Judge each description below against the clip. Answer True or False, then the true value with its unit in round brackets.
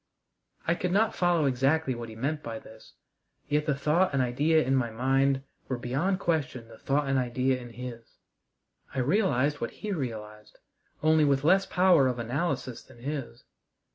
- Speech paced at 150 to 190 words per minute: True (170 wpm)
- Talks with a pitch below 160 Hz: True (135 Hz)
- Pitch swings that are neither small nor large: True (4.4 semitones)